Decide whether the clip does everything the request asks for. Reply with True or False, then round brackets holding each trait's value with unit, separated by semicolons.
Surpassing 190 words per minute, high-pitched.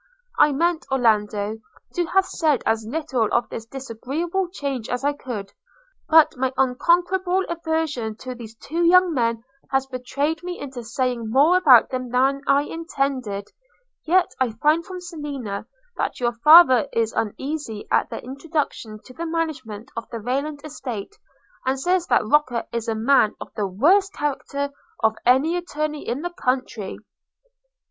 False (155 wpm; 270 Hz)